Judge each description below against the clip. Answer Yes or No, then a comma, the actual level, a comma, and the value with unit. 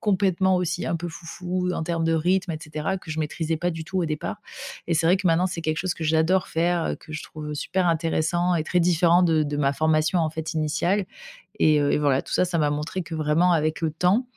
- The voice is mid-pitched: Yes, medium, 165 Hz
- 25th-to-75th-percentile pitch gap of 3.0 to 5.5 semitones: No, narrow, 2.4 semitones